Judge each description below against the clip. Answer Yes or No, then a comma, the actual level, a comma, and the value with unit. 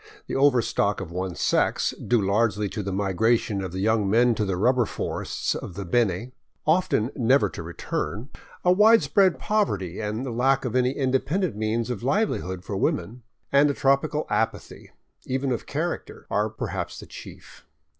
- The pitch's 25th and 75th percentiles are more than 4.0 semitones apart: Yes, average, 5.2 semitones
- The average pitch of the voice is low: Yes, low, 115 Hz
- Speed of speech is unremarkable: Yes, average, 165 wpm